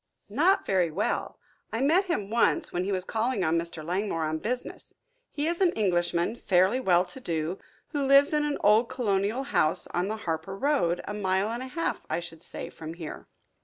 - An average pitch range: No, wide, 6.9 semitones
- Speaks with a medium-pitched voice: No, high, 200 Hz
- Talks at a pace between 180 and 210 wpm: Yes, average, 200 wpm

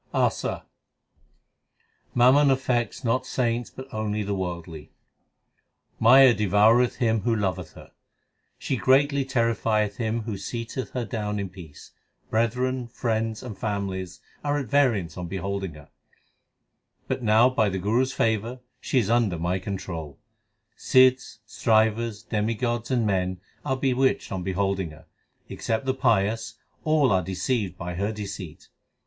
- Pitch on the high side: No, low, 110 Hz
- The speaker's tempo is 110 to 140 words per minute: Yes, slow, 135 wpm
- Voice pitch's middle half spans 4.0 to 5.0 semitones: Yes, average, 4.3 semitones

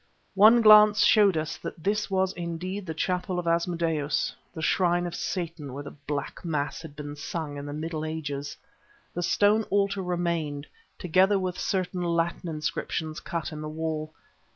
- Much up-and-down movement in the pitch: No, average, 3.3 semitones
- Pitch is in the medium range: Yes, medium, 170 Hz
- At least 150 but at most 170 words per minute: Yes, average, 165 wpm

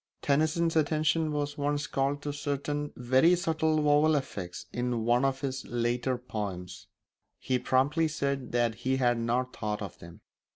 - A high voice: No, low, 135 Hz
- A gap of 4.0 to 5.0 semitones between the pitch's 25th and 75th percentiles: No, average, 3.5 semitones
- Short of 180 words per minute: Yes, average, 155 wpm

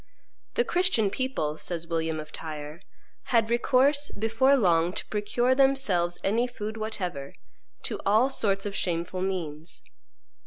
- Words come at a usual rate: No, slow, 130 wpm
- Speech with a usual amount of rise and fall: No, wide, 6.4 semitones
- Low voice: No, high, 200 Hz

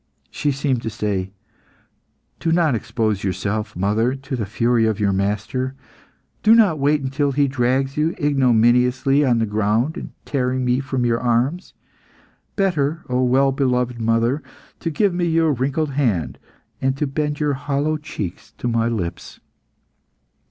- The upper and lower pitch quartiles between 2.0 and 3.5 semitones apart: No, average, 4.0 semitones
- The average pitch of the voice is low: Yes, low, 130 Hz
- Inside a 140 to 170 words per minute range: Yes, average, 150 wpm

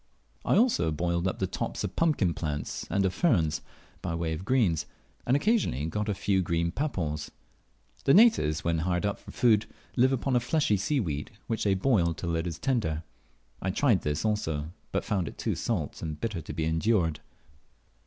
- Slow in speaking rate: No, average, 185 wpm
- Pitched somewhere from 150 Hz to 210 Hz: No, very low, 90 Hz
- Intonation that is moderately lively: No, wide, 6.1 semitones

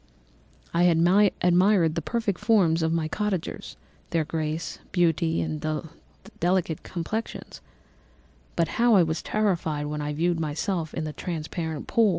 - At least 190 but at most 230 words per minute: No, slow, 135 wpm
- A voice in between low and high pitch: Yes, medium, 165 Hz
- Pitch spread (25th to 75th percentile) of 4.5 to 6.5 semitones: No, average, 2.8 semitones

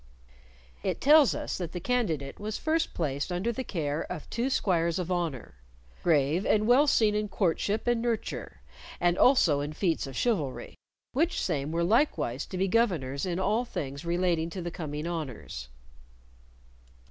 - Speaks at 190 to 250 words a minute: No, average, 160 wpm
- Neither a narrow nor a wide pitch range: No, wide, 6.4 semitones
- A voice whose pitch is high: No, medium, 175 Hz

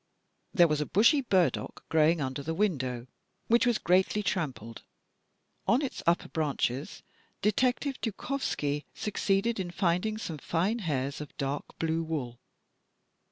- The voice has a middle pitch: Yes, medium, 170 Hz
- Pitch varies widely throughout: Yes, wide, 6.5 semitones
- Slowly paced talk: Yes, slow, 130 wpm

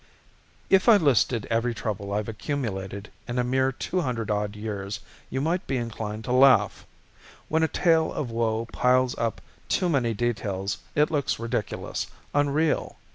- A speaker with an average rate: Yes, average, 160 wpm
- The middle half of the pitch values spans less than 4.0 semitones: No, average, 4.9 semitones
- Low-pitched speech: Yes, low, 120 Hz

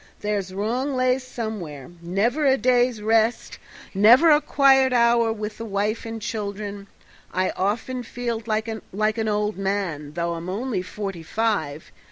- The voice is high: Yes, high, 215 Hz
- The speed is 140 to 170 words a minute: Yes, average, 145 wpm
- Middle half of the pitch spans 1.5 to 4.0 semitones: Yes, average, 3.4 semitones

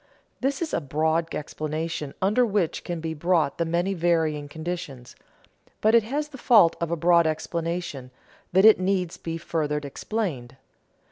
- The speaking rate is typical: Yes, average, 160 wpm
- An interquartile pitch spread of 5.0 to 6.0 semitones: No, average, 3.6 semitones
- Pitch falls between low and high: Yes, medium, 170 Hz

